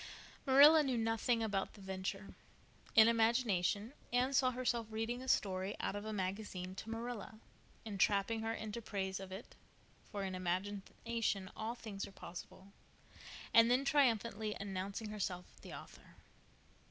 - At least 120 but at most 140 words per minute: Yes, slow, 135 wpm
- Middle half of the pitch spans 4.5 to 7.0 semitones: No, average, 3.2 semitones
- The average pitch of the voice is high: Yes, high, 215 Hz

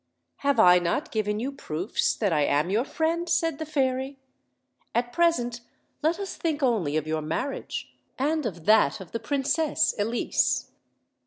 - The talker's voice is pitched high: Yes, high, 245 Hz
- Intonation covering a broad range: Yes, wide, 8.1 semitones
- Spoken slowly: No, average, 160 wpm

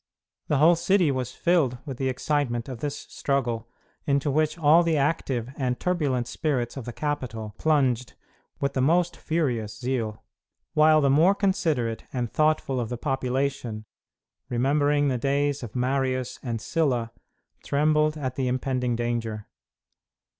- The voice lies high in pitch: No, low, 135 Hz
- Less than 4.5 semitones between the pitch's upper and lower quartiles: Yes, average, 3.7 semitones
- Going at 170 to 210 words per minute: No, average, 145 wpm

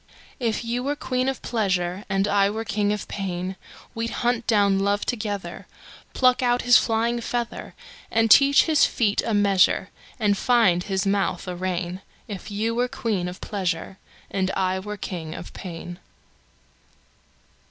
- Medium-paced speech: No, slow, 130 wpm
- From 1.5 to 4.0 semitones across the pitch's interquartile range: Yes, average, 3.7 semitones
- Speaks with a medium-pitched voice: No, high, 205 Hz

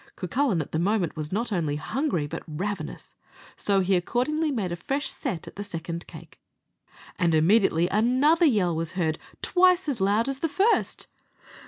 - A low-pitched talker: No, high, 200 Hz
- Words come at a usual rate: Yes, average, 170 wpm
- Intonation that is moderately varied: No, wide, 8.2 semitones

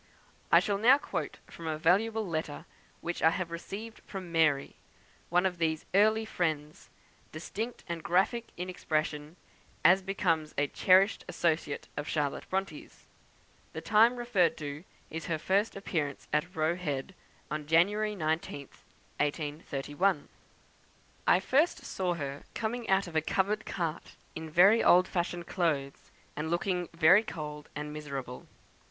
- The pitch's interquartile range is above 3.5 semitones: Yes, average, 4.2 semitones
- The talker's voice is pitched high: No, medium, 170 Hz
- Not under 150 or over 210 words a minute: No, average, 140 wpm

